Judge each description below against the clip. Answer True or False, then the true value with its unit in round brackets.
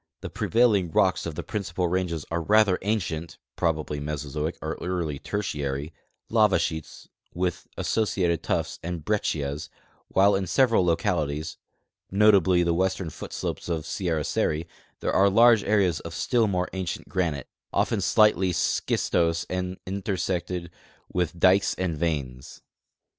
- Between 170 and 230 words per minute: False (140 wpm)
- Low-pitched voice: True (90 Hz)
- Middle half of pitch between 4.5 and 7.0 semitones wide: False (3.5 semitones)